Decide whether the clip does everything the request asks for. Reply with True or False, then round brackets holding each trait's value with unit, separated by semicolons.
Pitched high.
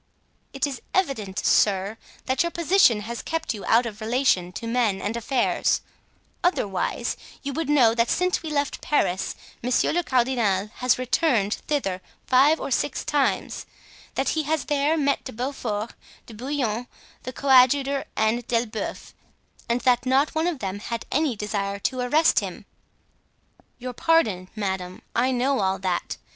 True (250 Hz)